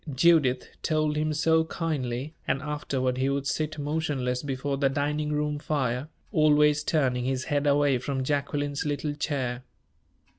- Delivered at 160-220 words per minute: No, average, 145 wpm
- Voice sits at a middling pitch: Yes, medium, 145 Hz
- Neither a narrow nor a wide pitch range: No, narrow, 2.3 semitones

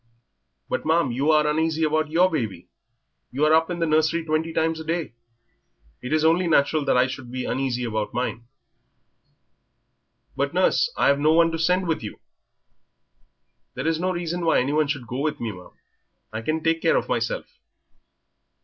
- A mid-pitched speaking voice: Yes, medium, 155 Hz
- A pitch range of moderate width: Yes, average, 3.9 semitones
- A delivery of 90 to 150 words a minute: No, average, 175 wpm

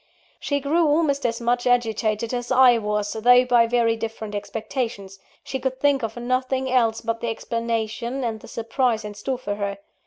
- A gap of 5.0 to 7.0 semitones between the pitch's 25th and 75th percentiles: No, narrow, 2.5 semitones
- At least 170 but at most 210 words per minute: Yes, average, 180 wpm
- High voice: Yes, high, 235 Hz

